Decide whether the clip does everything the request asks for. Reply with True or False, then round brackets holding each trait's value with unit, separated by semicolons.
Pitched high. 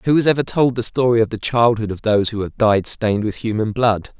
False (115 Hz)